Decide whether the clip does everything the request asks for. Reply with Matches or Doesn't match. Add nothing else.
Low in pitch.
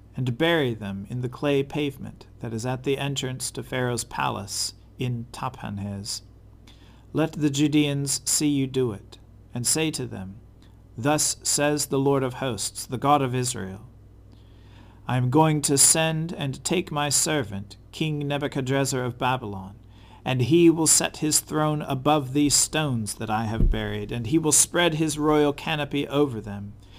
Matches